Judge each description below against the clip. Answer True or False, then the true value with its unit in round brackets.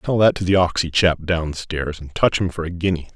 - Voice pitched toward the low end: True (85 Hz)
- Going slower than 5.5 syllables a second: True (5.3 syllables/s)